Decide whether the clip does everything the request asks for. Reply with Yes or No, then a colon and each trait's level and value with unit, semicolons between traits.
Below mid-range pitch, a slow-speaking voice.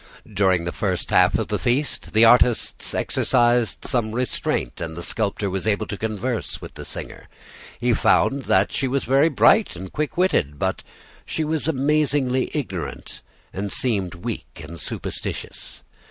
No: low, 115 Hz; average, 155 wpm